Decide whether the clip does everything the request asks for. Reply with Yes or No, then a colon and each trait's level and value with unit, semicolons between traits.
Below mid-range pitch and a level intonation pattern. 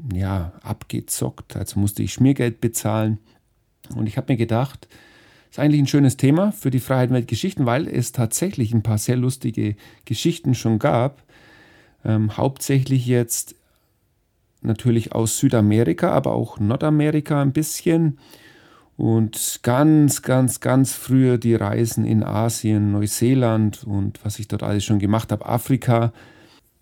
No: low, 120 Hz; average, 3.6 semitones